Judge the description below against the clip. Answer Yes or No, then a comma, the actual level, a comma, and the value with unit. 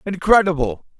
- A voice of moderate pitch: Yes, medium, 170 Hz